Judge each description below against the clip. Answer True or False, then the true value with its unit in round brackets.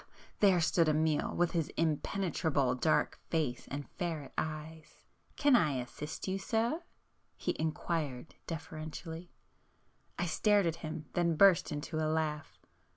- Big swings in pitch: False (2.4 semitones)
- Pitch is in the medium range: True (160 Hz)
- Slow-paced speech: True (125 wpm)